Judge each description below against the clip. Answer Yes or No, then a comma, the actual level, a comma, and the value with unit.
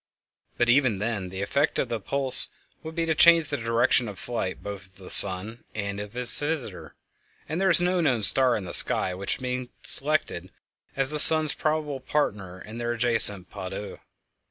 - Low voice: Yes, low, 120 Hz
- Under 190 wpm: No, average, 195 wpm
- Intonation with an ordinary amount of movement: No, wide, 6.4 semitones